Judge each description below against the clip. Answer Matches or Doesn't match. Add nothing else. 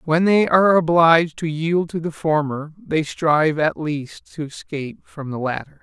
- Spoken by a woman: Doesn't match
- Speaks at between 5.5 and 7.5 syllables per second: Doesn't match